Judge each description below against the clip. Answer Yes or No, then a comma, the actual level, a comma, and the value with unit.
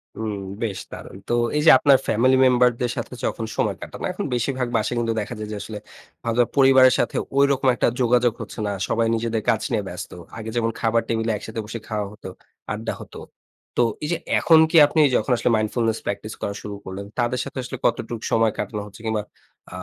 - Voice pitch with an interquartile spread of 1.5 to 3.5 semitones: Yes, narrow, 2.5 semitones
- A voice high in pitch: No, low, 115 Hz